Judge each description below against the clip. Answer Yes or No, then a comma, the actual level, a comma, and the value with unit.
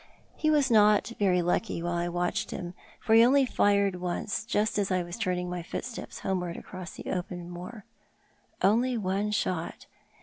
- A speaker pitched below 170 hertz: No, high, 190 Hz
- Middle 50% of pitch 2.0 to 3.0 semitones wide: No, average, 3.8 semitones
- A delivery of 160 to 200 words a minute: Yes, average, 170 wpm